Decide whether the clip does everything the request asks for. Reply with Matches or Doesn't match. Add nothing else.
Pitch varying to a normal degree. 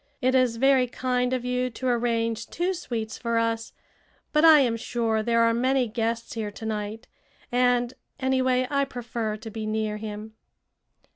Doesn't match